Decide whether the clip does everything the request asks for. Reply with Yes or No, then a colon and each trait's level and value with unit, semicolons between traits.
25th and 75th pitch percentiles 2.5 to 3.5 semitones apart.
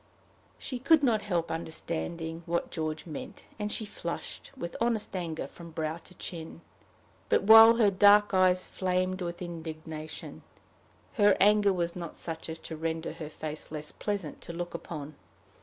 No: average, 4.0 semitones